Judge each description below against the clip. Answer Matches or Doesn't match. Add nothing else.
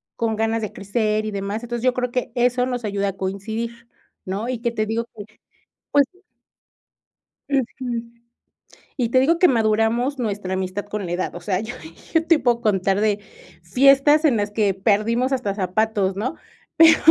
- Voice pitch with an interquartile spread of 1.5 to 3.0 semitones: Doesn't match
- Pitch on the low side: Doesn't match